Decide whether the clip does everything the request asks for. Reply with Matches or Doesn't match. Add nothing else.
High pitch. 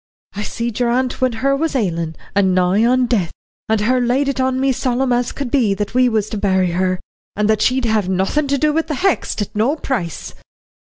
Matches